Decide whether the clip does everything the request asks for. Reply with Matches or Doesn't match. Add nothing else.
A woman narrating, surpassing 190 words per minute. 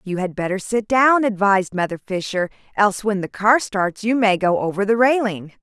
Matches